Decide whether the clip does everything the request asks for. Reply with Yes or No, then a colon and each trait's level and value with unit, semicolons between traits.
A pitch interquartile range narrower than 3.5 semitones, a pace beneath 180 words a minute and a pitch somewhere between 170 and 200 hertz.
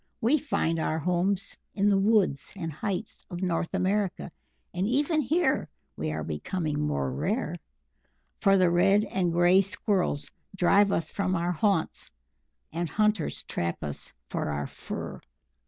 No: average, 3.8 semitones; average, 145 wpm; medium, 185 Hz